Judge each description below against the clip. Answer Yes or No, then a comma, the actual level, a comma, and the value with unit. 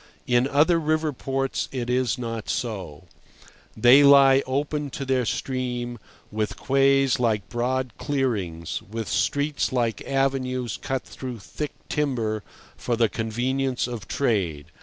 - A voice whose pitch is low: Yes, low, 125 Hz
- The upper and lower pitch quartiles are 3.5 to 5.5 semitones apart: No, average, 3.1 semitones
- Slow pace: Yes, slow, 130 wpm